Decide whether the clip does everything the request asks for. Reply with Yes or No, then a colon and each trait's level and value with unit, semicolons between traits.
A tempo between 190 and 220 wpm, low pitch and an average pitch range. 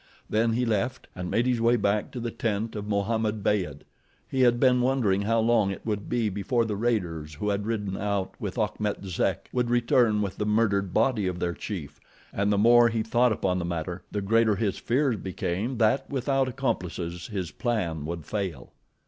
Yes: average, 195 wpm; low, 105 Hz; average, 3.5 semitones